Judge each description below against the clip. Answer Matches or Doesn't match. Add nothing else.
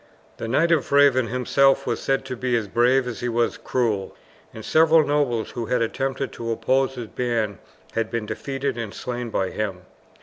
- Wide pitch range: Doesn't match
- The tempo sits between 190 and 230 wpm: Matches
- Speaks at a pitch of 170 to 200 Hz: Doesn't match